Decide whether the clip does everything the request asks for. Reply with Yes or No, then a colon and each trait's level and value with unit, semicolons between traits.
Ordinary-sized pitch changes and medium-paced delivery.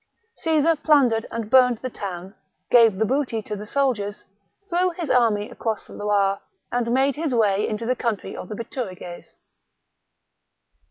Yes: average, 4.2 semitones; average, 155 wpm